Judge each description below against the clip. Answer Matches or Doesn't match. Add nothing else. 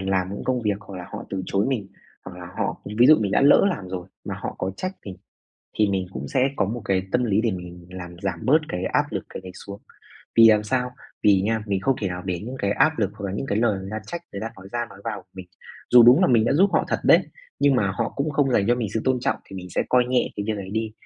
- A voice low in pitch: Matches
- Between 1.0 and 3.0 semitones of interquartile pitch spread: Doesn't match